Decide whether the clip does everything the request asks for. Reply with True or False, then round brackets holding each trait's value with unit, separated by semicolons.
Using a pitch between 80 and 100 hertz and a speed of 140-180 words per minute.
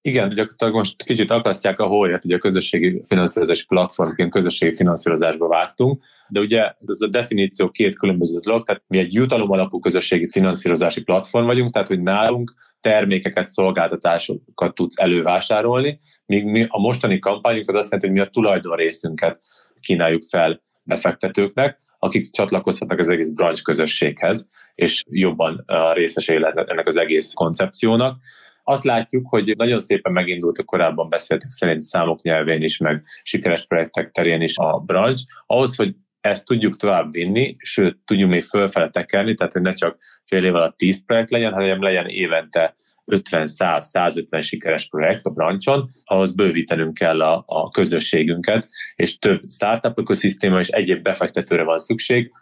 True (95 Hz; 150 wpm)